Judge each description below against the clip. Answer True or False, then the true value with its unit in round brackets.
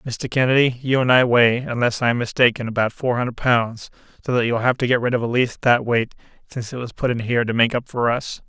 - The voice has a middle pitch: False (120 Hz)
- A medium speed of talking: False (255 wpm)